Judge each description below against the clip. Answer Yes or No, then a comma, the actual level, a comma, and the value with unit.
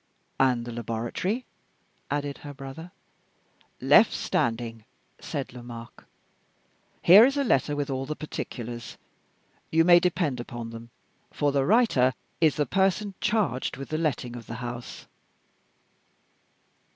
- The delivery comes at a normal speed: No, slow, 125 wpm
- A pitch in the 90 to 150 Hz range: Yes, low, 135 Hz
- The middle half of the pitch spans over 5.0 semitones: Yes, wide, 5.6 semitones